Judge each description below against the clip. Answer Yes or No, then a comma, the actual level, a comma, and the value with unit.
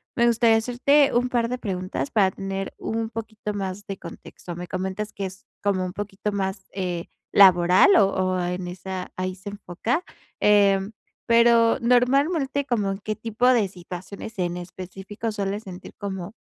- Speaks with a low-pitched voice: No, high, 200 Hz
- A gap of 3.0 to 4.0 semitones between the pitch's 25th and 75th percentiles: Yes, average, 3.5 semitones